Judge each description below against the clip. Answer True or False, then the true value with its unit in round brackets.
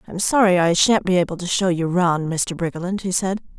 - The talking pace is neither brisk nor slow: False (235 wpm)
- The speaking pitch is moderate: True (180 Hz)